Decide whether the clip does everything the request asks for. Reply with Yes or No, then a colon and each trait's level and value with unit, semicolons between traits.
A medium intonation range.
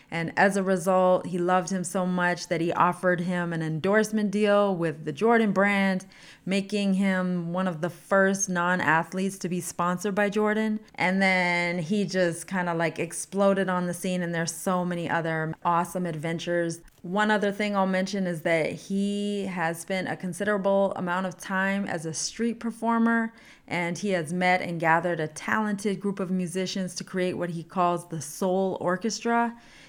No: narrow, 2.2 semitones